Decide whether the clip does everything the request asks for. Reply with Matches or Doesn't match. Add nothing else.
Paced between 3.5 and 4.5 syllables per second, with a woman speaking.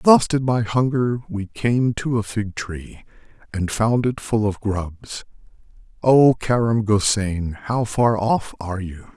Doesn't match